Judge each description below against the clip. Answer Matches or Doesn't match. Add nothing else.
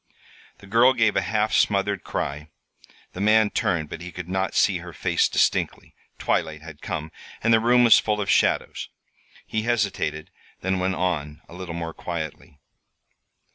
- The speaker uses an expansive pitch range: Doesn't match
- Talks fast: Doesn't match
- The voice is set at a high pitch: Doesn't match